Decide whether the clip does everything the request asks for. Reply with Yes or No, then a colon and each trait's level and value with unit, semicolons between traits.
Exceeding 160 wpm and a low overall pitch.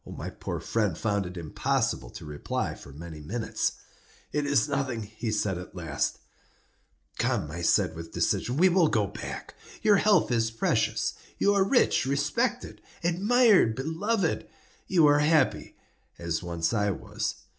No: average, 150 wpm; low, 120 Hz